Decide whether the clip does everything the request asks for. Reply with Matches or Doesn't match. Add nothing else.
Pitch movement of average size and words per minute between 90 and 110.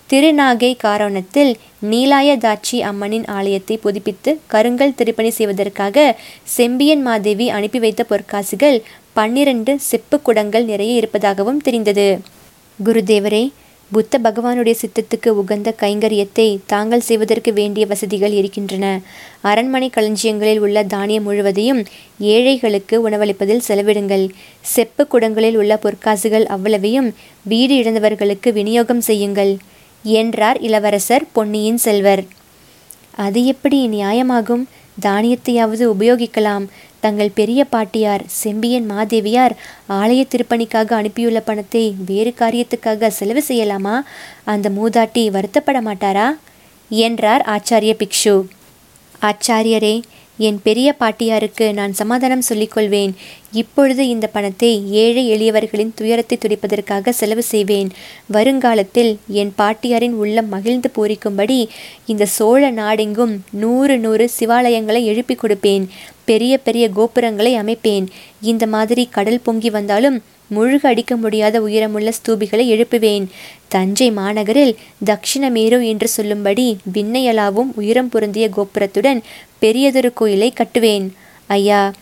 Doesn't match